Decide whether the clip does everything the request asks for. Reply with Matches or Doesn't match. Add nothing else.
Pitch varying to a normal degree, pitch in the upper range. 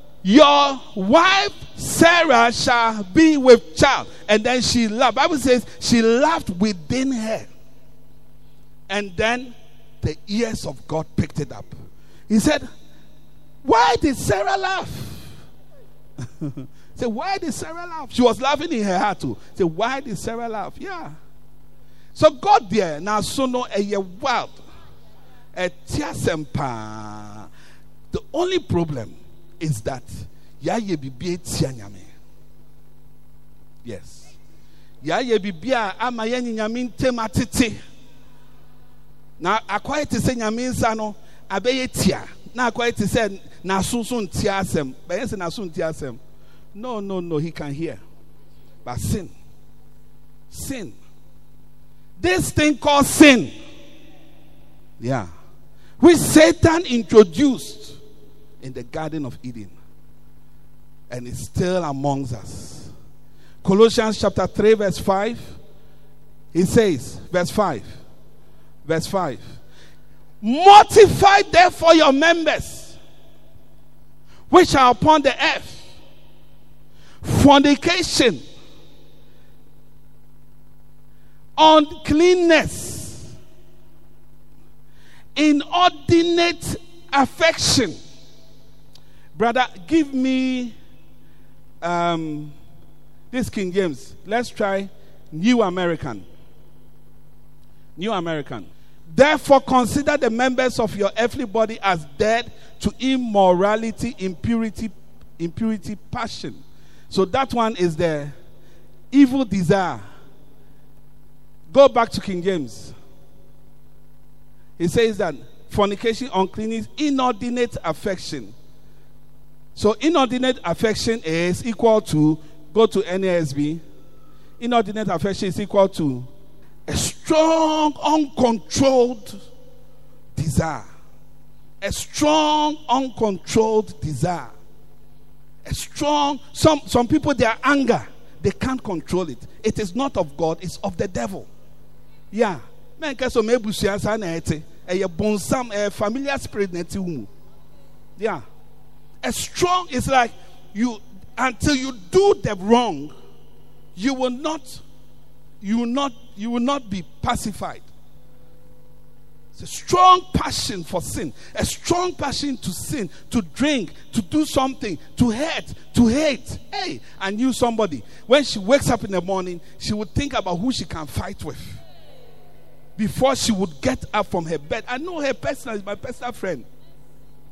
Doesn't match